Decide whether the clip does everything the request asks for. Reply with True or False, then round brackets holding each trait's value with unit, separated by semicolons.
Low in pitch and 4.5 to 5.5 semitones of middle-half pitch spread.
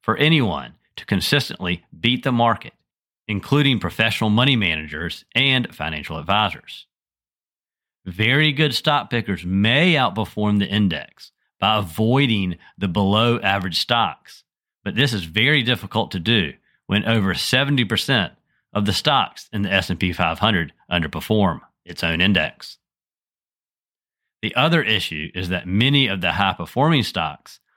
True (105 Hz; 4.9 semitones)